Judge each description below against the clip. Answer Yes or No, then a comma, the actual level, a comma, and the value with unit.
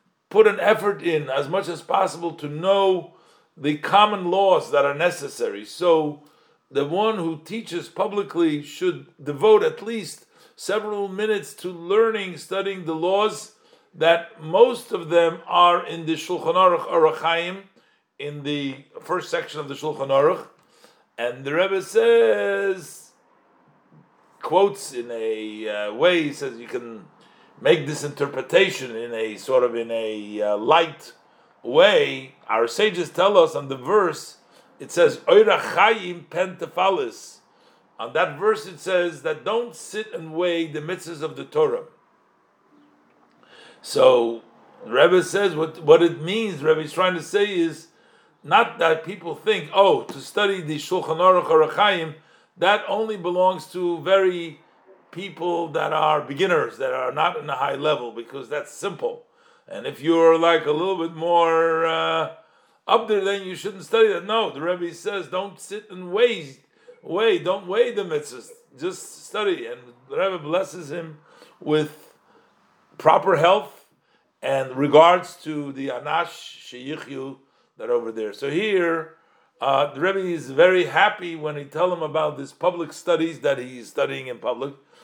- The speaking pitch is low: No, medium, 175 Hz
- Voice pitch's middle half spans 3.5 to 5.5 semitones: Yes, average, 5.1 semitones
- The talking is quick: No, average, 150 wpm